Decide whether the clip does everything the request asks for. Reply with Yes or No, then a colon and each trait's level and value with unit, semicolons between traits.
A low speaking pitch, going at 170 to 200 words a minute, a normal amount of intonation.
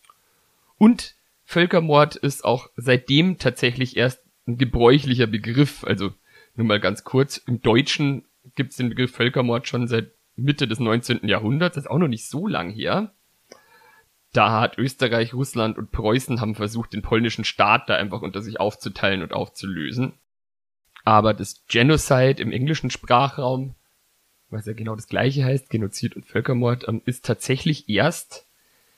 No: low, 120 Hz; average, 150 wpm; average, 3.5 semitones